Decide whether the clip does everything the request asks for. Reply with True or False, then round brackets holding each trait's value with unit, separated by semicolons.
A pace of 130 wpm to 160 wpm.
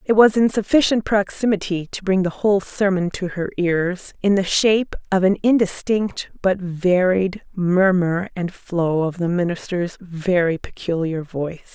True (155 wpm)